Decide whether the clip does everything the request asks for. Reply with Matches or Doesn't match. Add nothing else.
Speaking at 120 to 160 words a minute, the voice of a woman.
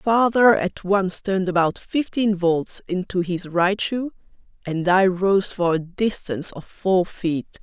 Matches